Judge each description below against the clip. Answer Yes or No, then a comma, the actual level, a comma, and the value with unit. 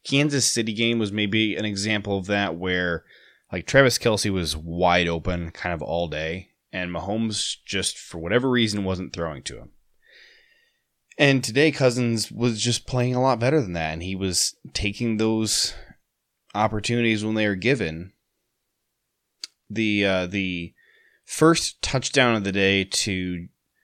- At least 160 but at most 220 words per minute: No, average, 150 wpm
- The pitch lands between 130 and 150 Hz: No, low, 105 Hz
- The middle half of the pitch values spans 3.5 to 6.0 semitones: Yes, average, 4.9 semitones